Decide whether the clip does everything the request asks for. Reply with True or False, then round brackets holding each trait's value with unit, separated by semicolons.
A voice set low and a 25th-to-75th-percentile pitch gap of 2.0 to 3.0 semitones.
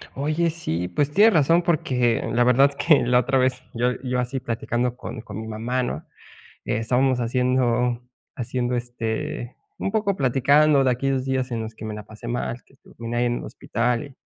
True (125 Hz; 2.4 semitones)